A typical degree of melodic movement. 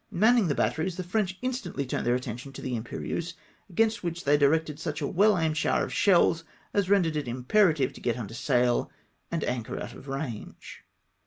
No: wide, 6.0 semitones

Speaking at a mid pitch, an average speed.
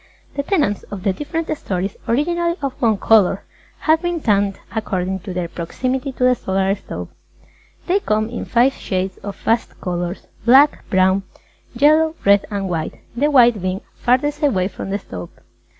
No: high, 215 Hz; average, 165 wpm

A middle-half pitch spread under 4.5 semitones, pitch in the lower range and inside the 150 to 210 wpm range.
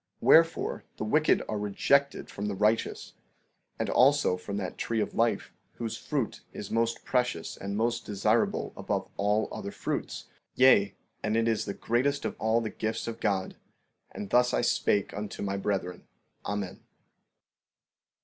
Yes: average, 2.8 semitones; low, 110 Hz; average, 160 wpm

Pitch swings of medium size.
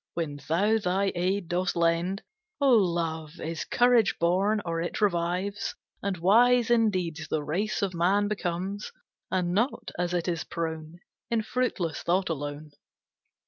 Yes: average, 3.4 semitones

